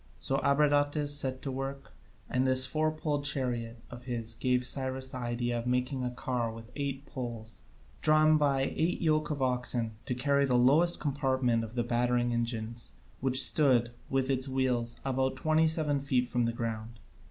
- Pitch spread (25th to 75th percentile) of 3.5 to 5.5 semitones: No, average, 2.7 semitones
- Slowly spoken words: No, average, 175 wpm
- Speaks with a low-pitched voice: Yes, low, 130 Hz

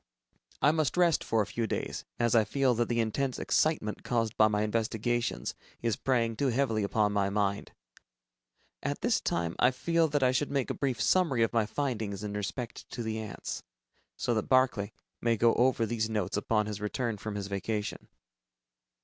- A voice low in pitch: Yes, low, 115 Hz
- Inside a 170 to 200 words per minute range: Yes, average, 185 wpm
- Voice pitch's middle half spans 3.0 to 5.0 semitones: Yes, average, 3.3 semitones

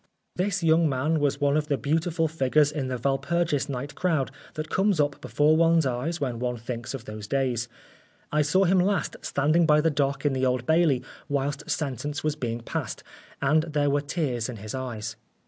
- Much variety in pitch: No, average, 3.6 semitones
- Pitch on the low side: No, medium, 145 Hz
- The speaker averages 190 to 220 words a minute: Yes, average, 195 wpm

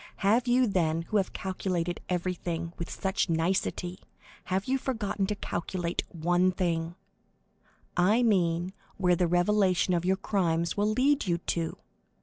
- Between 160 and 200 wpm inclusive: No, slow, 135 wpm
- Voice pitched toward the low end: No, medium, 185 Hz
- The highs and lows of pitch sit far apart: No, average, 2.9 semitones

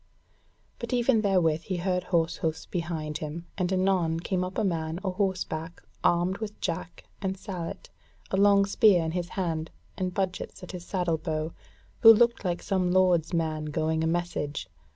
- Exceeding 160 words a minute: Yes, average, 170 wpm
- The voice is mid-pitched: Yes, medium, 180 Hz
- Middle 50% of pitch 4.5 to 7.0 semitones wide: No, average, 2.8 semitones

